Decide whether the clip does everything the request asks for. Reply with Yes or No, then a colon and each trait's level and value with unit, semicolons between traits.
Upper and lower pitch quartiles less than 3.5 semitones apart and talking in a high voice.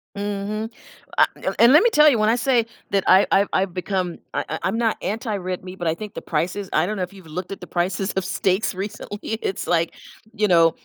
Yes: average, 2.8 semitones; high, 195 Hz